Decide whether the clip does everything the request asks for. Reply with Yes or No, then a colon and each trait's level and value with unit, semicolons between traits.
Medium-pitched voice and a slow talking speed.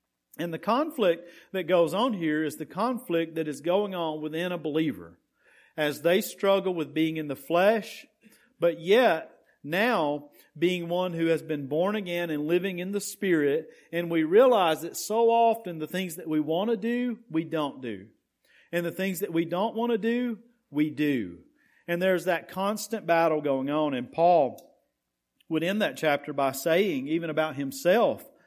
No: medium, 170 Hz; average, 180 wpm